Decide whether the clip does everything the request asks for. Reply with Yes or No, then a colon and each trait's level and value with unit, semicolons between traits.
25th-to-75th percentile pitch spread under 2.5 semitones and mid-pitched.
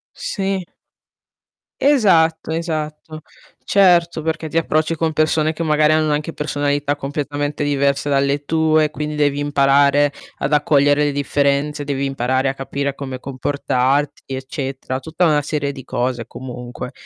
Yes: narrow, 2.1 semitones; medium, 145 Hz